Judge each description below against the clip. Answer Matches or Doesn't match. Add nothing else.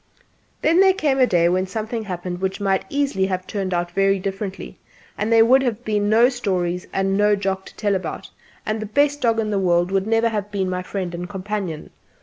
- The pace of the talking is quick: Matches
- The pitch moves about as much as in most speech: Matches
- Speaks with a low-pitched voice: Doesn't match